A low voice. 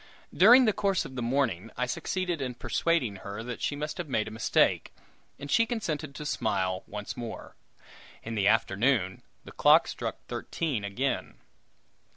Yes: low, 125 Hz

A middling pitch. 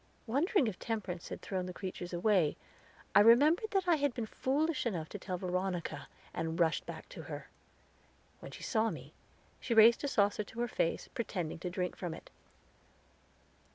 No: high, 210 Hz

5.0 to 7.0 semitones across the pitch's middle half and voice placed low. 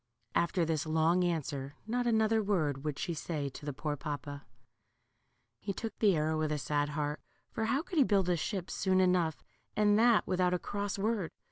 No: wide, 5.4 semitones; medium, 175 Hz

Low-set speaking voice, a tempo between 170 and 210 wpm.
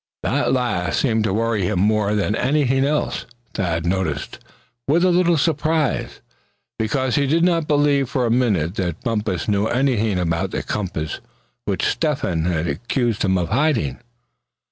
No: low, 110 Hz; average, 155 wpm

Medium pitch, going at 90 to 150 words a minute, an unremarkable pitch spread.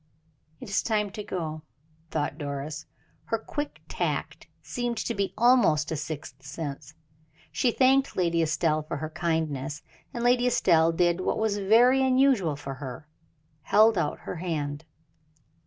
No: medium, 170 Hz; average, 145 wpm; wide, 6.4 semitones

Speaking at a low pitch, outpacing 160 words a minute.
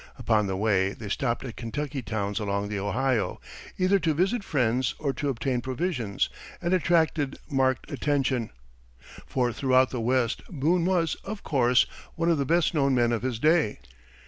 Yes: low, 130 Hz; average, 170 wpm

